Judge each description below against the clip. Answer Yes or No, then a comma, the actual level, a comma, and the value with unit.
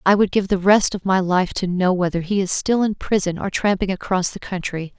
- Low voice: No, high, 190 Hz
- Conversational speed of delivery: No, fast, 255 wpm